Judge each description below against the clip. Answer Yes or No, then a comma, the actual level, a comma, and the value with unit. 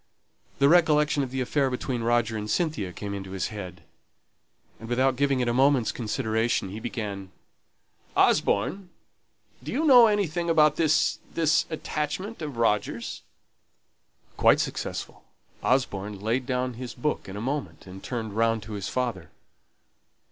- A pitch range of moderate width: No, wide, 5.8 semitones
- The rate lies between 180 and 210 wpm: No, average, 145 wpm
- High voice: No, low, 125 Hz